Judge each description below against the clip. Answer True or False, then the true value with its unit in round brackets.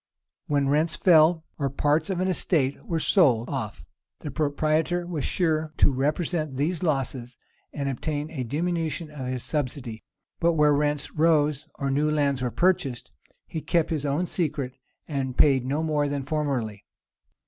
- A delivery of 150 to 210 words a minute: True (160 wpm)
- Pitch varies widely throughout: False (2.8 semitones)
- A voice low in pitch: False (150 Hz)